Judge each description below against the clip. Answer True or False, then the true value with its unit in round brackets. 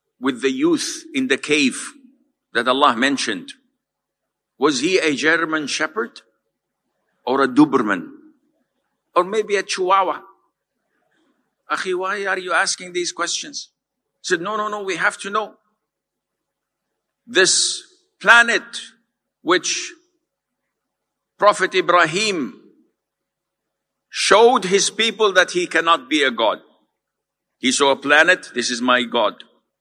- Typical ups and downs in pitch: False (7.5 semitones)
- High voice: True (215 Hz)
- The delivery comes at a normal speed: True (120 wpm)